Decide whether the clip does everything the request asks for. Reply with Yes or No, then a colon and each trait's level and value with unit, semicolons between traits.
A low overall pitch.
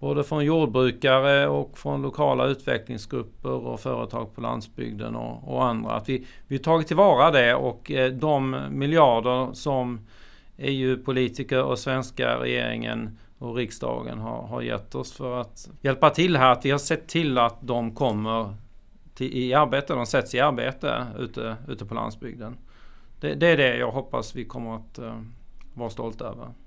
Yes: low, 125 Hz